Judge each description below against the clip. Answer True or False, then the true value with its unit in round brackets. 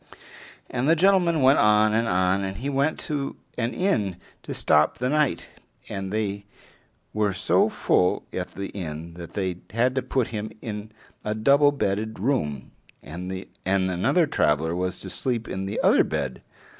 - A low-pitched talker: True (105 Hz)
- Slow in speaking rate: False (165 wpm)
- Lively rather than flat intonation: True (5.9 semitones)